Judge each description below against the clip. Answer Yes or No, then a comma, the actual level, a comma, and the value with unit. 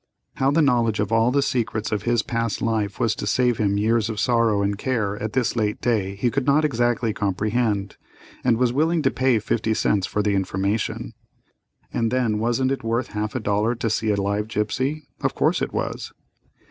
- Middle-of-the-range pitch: No, low, 115 Hz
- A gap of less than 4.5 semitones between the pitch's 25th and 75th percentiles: Yes, average, 2.8 semitones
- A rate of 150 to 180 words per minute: No, average, 200 wpm